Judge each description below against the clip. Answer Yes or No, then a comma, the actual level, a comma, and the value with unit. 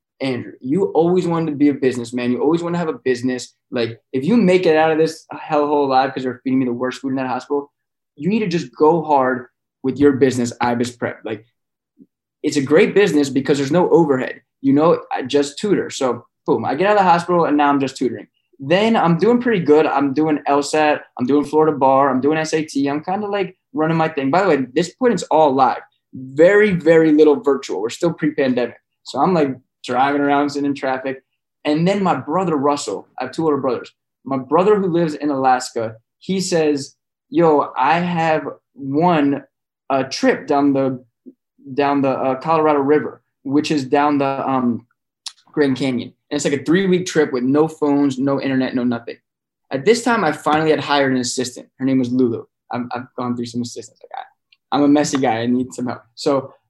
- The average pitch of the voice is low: No, medium, 145 Hz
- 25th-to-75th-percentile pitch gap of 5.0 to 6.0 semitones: No, average, 3.4 semitones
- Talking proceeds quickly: Yes, fast, 215 wpm